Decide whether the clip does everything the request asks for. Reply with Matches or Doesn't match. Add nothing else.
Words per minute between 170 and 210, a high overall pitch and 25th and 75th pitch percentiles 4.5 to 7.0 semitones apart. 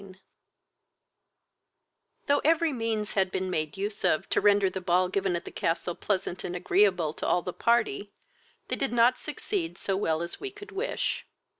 Matches